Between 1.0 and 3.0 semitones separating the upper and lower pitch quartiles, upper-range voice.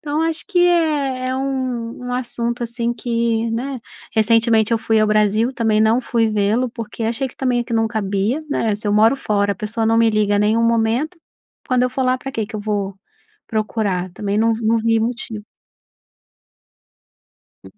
Yes: narrow, 2.6 semitones; high, 230 Hz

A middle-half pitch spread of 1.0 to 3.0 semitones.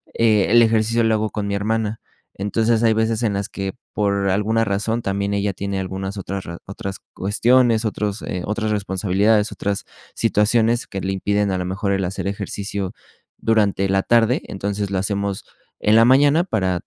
Yes: narrow, 2.4 semitones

